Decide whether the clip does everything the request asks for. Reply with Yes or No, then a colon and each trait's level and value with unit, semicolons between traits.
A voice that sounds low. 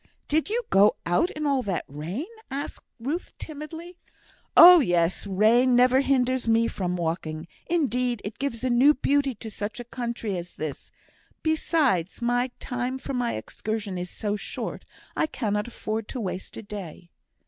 No: high, 240 Hz